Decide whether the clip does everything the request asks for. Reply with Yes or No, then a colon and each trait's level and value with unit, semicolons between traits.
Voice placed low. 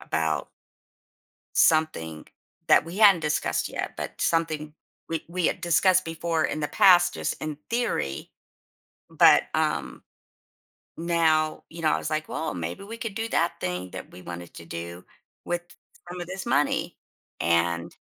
No: medium, 160 Hz